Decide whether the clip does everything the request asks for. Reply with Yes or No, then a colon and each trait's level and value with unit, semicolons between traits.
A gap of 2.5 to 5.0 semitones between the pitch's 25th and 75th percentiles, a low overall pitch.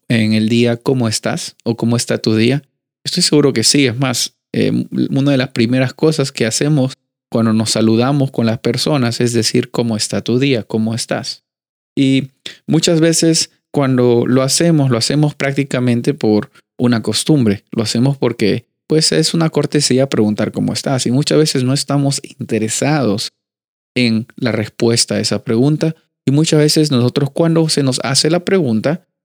Yes: average, 3.9 semitones; low, 130 Hz